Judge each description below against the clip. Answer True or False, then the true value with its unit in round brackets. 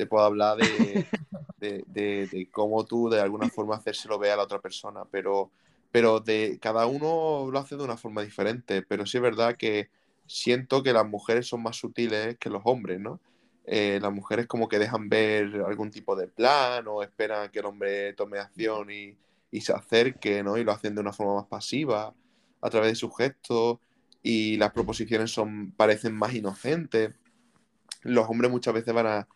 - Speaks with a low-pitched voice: True (110 Hz)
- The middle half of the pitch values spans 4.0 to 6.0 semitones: False (2.4 semitones)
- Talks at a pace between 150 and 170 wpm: False (190 wpm)